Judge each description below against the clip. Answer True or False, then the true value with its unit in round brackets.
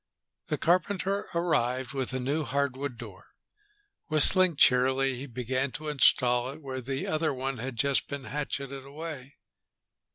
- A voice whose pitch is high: False (135 Hz)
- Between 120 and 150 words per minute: True (140 wpm)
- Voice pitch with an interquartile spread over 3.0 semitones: False (2.7 semitones)